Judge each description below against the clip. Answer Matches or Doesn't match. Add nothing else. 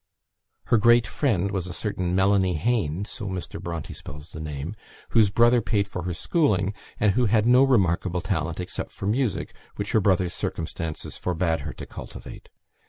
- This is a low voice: Matches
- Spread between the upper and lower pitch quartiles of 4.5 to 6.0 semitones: Doesn't match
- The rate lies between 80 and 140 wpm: Doesn't match